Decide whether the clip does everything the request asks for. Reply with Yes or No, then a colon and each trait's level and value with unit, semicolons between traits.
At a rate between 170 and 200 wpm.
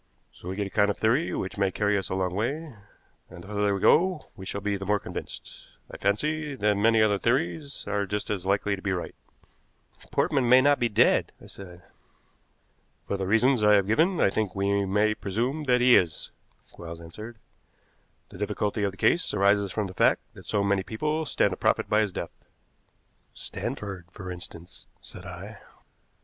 Yes: average, 195 wpm